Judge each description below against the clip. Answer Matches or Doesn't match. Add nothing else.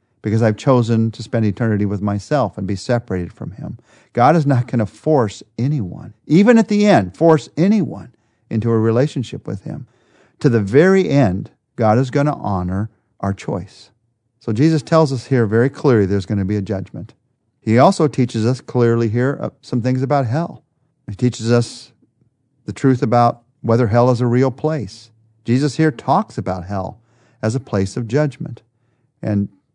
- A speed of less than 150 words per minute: Doesn't match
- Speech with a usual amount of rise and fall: Matches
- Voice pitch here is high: Doesn't match